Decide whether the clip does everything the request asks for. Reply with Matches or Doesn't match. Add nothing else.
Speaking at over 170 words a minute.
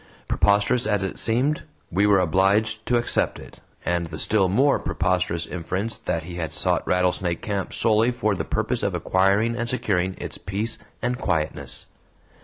Doesn't match